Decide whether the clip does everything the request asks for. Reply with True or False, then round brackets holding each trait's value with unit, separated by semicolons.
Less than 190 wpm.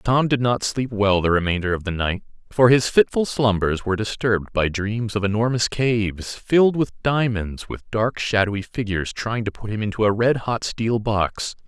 False (195 wpm)